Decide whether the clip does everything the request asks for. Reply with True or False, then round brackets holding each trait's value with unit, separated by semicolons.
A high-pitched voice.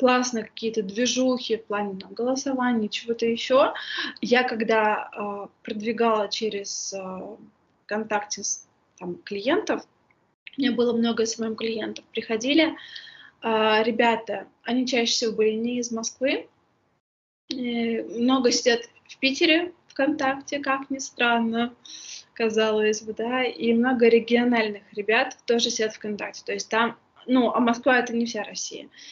True (235 Hz)